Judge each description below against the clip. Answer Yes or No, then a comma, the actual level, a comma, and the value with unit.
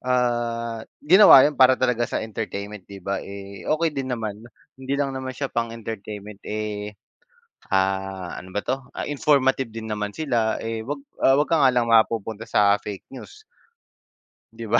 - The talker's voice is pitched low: Yes, low, 115 Hz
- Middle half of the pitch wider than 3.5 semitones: Yes, average, 4.1 semitones